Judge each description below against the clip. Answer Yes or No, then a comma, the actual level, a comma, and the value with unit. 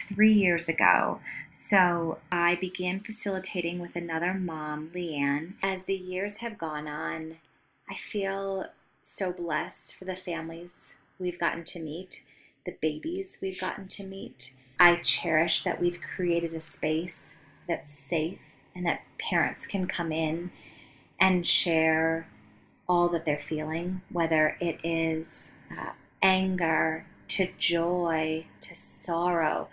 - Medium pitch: Yes, medium, 170 Hz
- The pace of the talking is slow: Yes, slow, 130 wpm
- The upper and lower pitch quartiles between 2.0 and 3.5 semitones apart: Yes, narrow, 2.6 semitones